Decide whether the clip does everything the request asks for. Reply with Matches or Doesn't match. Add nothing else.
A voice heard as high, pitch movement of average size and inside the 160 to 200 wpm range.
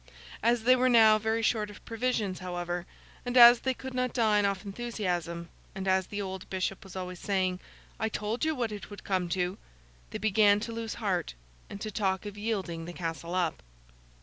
Matches